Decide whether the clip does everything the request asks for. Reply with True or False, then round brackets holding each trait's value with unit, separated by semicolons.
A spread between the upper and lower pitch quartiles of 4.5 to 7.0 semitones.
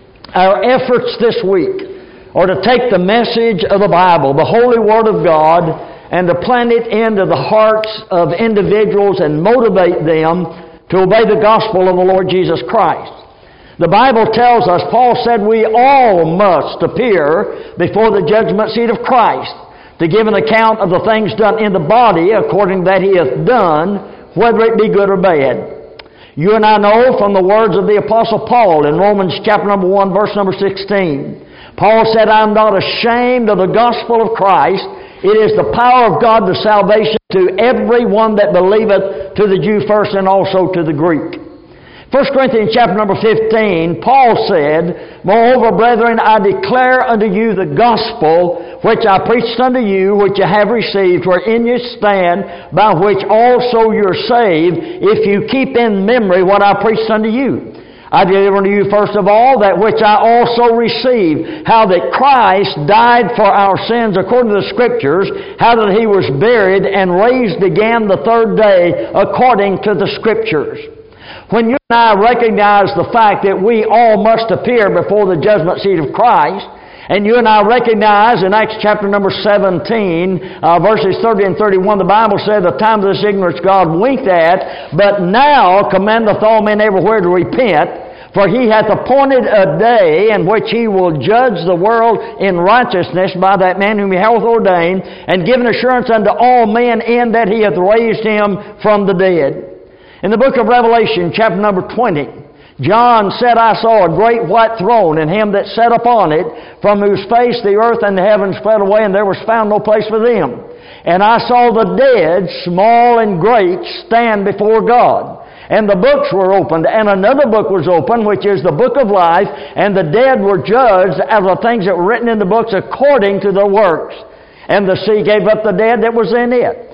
False (3.2 semitones)